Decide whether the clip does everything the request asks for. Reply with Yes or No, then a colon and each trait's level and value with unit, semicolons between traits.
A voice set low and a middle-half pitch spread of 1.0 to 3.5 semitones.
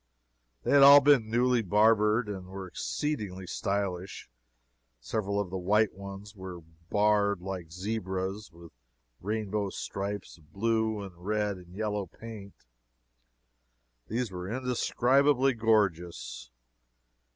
Yes: low, 105 Hz; average, 2.9 semitones